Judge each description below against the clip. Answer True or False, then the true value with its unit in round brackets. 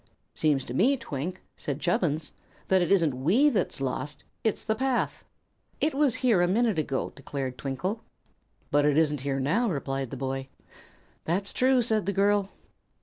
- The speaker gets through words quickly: False (165 wpm)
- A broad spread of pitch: True (7.8 semitones)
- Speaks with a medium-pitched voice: True (170 Hz)